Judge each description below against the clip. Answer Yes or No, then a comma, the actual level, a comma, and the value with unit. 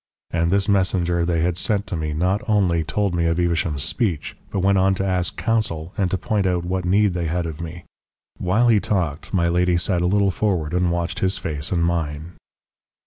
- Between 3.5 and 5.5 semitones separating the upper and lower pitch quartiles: No, narrow, 2.5 semitones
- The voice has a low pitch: Yes, very low, 90 Hz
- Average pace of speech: No, fast, 210 wpm